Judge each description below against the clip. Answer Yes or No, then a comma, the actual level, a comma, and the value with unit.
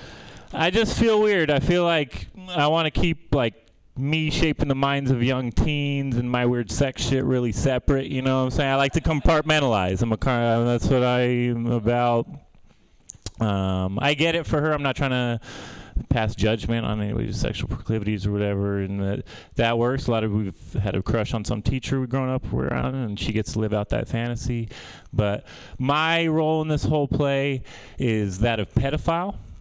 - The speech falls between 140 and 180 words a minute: No, average, 200 wpm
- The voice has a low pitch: Yes, low, 125 Hz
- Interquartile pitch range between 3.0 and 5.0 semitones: Yes, average, 4.4 semitones